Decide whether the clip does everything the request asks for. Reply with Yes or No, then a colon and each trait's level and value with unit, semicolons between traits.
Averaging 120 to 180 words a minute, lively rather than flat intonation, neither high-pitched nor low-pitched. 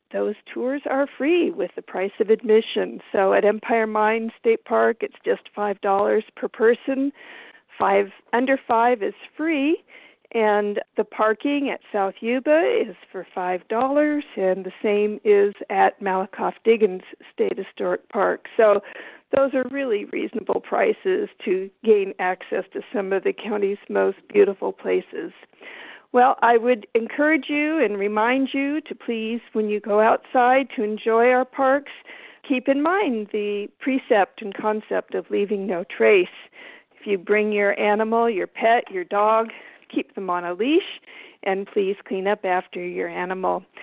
No: average, 155 wpm; wide, 5.8 semitones; high, 225 Hz